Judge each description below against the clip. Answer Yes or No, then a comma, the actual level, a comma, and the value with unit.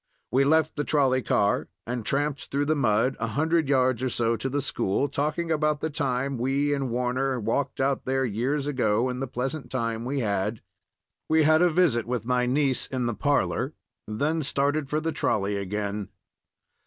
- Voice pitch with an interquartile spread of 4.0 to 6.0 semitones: No, average, 3.5 semitones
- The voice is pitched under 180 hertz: Yes, low, 135 Hz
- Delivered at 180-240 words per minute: Yes, average, 185 wpm